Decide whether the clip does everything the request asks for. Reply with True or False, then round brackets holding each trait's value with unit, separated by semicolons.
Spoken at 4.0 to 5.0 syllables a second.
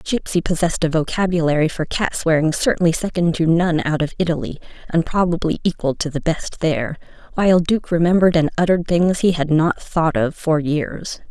False (5.6 syllables/s)